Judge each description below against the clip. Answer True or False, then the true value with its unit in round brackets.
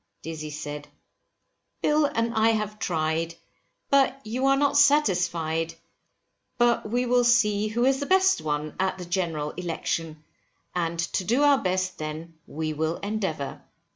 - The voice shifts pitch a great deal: True (7.0 semitones)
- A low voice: False (185 Hz)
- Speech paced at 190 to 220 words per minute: False (145 wpm)